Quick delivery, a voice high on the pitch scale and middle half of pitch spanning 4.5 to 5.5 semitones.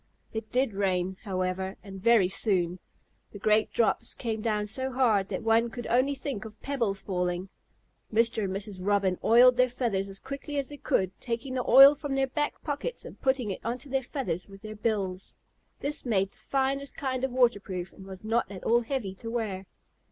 No: average, 195 wpm; high, 225 Hz; average, 5.0 semitones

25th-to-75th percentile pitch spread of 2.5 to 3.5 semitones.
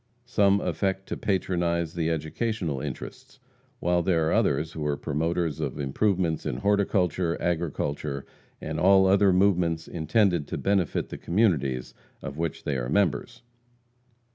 No: average, 3.9 semitones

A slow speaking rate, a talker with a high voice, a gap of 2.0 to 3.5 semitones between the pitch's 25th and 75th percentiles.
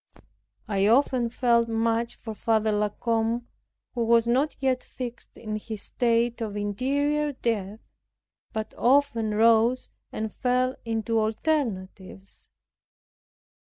Yes: slow, 115 wpm; high, 230 Hz; narrow, 2.5 semitones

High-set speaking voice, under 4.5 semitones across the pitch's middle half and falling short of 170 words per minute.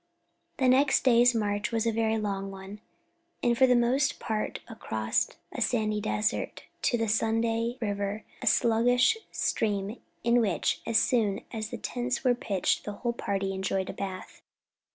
Yes: high, 225 Hz; average, 2.9 semitones; average, 160 wpm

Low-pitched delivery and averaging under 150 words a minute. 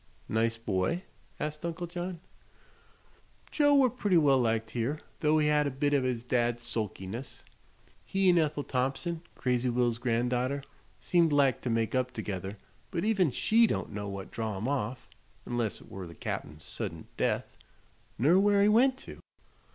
No: low, 130 Hz; average, 165 wpm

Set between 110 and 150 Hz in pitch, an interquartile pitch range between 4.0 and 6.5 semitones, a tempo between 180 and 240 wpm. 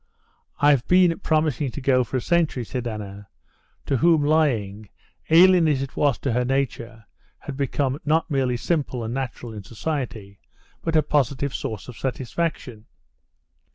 No: low, 135 Hz; average, 4.4 semitones; average, 155 wpm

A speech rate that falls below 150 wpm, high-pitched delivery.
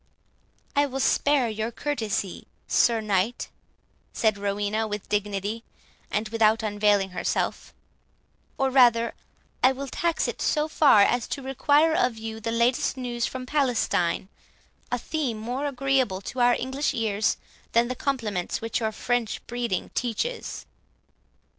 Yes: slow, 135 wpm; high, 235 Hz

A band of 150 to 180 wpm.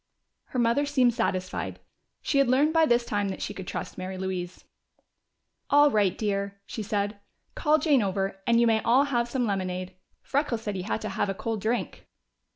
No: average, 190 wpm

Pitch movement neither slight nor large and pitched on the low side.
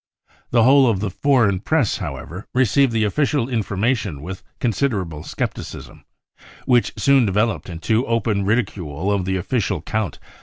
Yes: average, 4.6 semitones; low, 110 Hz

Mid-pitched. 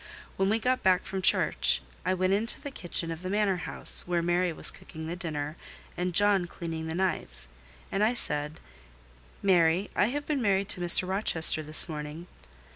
Yes: medium, 180 Hz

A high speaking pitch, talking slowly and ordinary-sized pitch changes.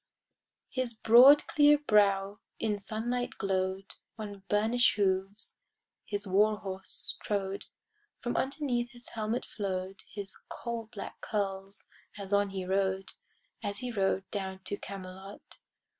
Yes: high, 205 Hz; slow, 125 wpm; average, 3.0 semitones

